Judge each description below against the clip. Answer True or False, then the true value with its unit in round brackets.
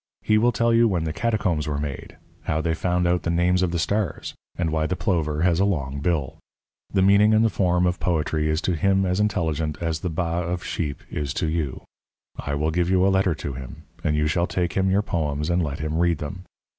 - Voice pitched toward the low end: True (85 Hz)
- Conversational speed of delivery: False (240 wpm)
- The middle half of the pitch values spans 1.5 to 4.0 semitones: True (3.4 semitones)